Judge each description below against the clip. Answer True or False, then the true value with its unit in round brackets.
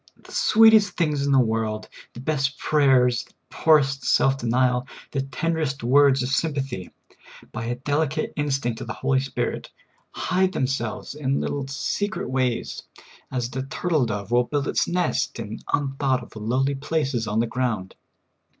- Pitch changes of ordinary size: True (3.1 semitones)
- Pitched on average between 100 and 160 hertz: True (135 Hz)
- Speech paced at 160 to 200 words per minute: True (170 wpm)